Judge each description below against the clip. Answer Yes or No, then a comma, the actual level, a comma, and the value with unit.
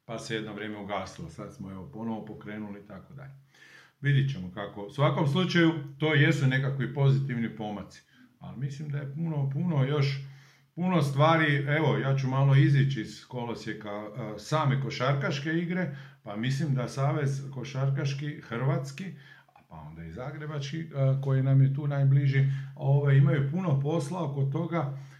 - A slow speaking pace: No, average, 150 wpm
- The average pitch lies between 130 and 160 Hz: Yes, low, 135 Hz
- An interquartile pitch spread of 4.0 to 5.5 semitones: No, average, 3.2 semitones